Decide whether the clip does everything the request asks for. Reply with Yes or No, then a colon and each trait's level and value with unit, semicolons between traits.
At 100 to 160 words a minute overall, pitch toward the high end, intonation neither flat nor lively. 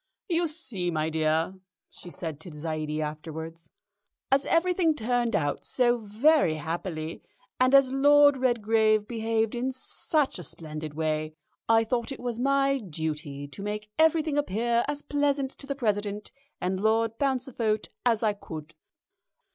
No: average, 145 wpm; high, 220 Hz; wide, 8.7 semitones